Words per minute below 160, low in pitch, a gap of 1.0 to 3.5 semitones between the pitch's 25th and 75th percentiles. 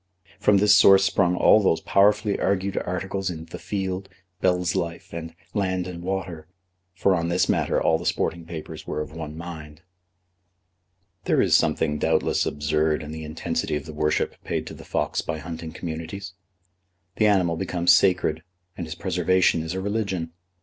No: average, 170 wpm; very low, 85 Hz; average, 3.0 semitones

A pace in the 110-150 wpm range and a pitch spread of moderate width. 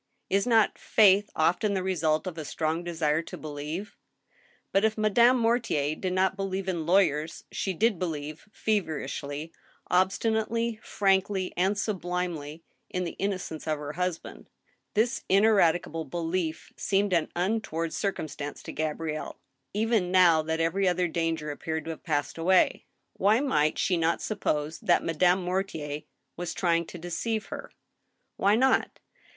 Yes: average, 145 wpm; average, 3.8 semitones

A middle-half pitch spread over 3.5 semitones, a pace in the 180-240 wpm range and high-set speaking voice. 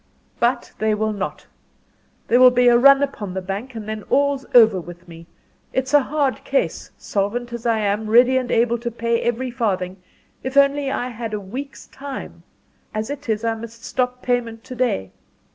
No: average, 3.2 semitones; average, 190 wpm; high, 235 Hz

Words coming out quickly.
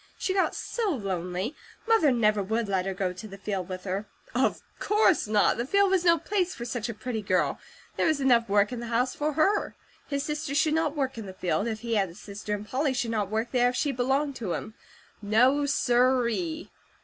Yes: fast, 225 wpm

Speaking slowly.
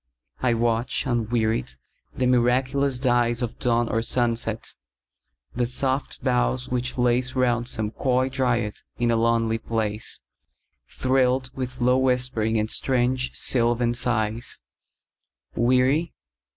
Yes: slow, 100 wpm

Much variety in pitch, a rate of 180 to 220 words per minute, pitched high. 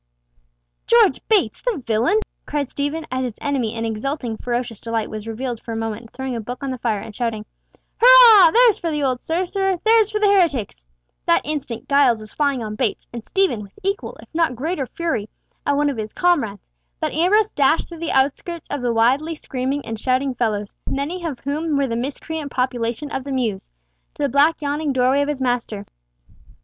Yes: wide, 5.7 semitones; average, 195 wpm; very high, 270 Hz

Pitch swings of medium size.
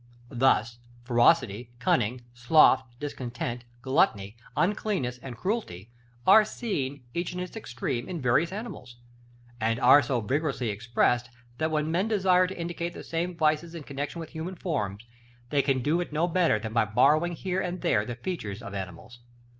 No: wide, 6.4 semitones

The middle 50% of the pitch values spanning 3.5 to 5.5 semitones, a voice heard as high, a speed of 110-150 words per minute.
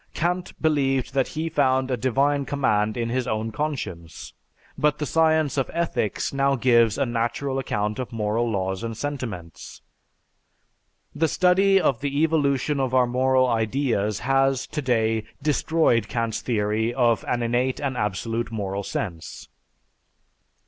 No: average, 4.0 semitones; low, 125 Hz; average, 140 wpm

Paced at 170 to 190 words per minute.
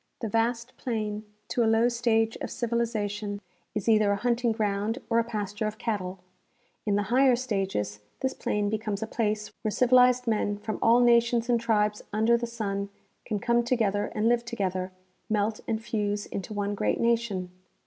Yes: average, 175 wpm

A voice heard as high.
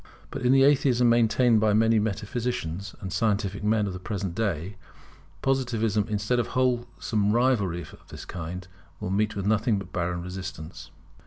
No: low, 105 Hz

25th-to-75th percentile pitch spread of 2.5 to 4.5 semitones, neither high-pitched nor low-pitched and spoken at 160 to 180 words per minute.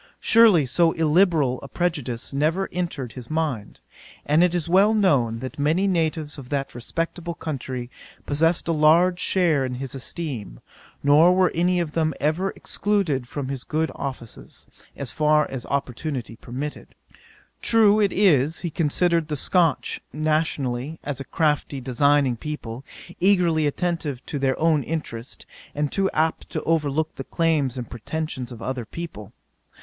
No: average, 4.1 semitones; medium, 150 Hz; average, 150 wpm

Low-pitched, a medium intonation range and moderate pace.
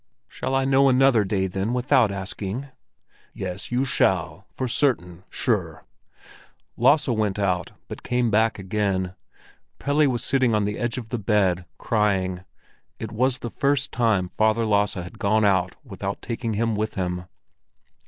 Yes: low, 110 Hz; average, 4.3 semitones; average, 150 wpm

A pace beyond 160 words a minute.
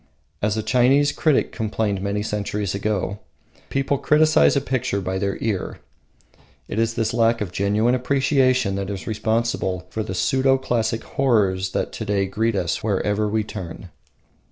No: average, 155 wpm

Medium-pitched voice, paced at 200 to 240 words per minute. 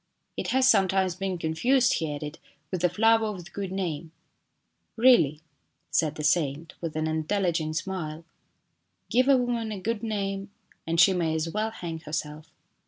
No: medium, 180 Hz; average, 185 wpm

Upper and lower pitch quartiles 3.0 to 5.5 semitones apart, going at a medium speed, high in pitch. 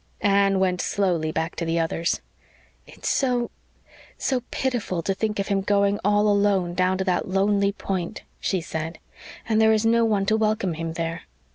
Yes: average, 3.3 semitones; average, 175 wpm; high, 195 Hz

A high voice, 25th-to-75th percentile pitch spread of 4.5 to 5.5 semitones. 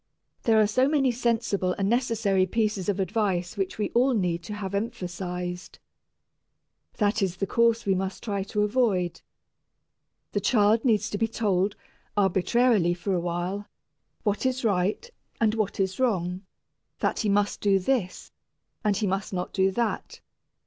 No: high, 205 Hz; average, 3.4 semitones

